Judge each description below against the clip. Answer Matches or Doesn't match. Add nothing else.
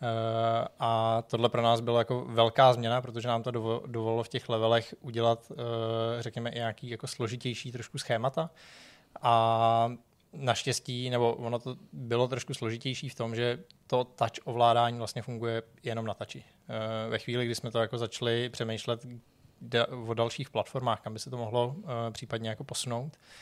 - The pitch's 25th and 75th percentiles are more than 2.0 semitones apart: Doesn't match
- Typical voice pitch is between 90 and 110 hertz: Doesn't match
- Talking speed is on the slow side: Doesn't match